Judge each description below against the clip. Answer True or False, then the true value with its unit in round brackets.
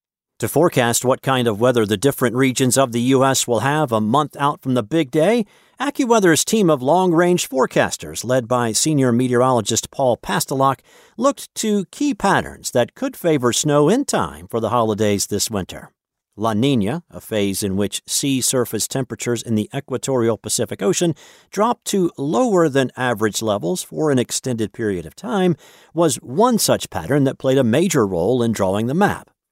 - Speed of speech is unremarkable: True (175 wpm)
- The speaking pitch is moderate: False (130 Hz)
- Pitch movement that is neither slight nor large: False (6.7 semitones)